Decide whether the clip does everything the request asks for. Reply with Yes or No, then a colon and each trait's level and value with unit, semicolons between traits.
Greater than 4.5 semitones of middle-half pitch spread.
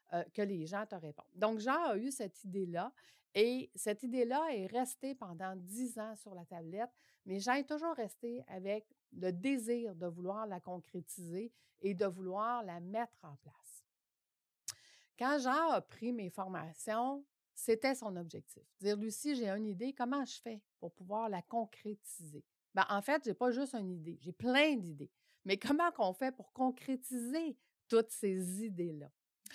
Yes: average, 5.0 semitones